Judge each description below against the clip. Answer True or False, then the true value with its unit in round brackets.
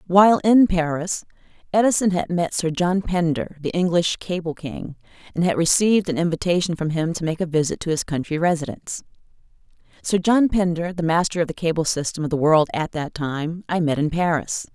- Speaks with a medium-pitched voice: True (170 Hz)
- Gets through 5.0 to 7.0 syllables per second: True (5.5 syllables/s)